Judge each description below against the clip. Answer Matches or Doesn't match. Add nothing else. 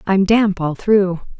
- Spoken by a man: Doesn't match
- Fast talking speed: Doesn't match